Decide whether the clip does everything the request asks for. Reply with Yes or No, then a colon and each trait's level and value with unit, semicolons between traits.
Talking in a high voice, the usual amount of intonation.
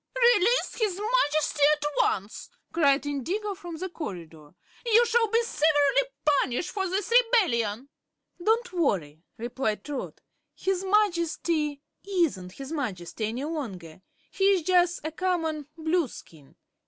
No: very high, 320 Hz; wide, 7.7 semitones